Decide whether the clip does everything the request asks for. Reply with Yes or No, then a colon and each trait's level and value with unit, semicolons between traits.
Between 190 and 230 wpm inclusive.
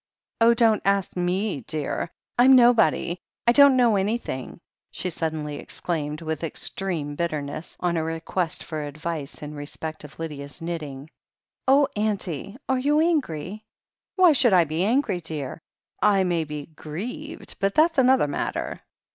No: average, 150 wpm